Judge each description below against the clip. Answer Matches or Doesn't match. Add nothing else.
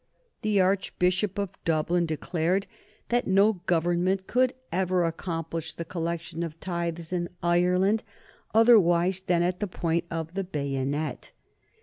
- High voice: Doesn't match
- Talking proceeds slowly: Matches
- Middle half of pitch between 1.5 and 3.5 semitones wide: Matches